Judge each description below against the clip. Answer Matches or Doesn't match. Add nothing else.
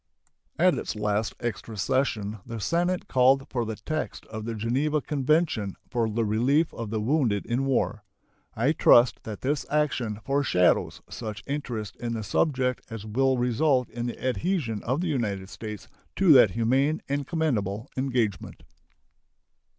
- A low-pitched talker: Matches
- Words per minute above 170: Doesn't match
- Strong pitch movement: Doesn't match